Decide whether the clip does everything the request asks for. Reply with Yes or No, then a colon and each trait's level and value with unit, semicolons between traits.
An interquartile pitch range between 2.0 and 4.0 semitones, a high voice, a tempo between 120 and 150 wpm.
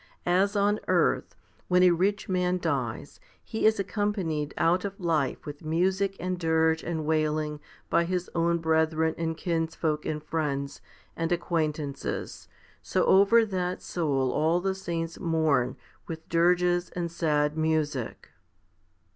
No: average, 2.7 semitones; medium, 165 Hz; slow, 135 wpm